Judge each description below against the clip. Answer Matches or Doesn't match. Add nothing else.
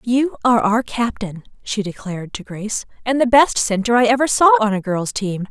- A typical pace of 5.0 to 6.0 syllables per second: Matches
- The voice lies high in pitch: Matches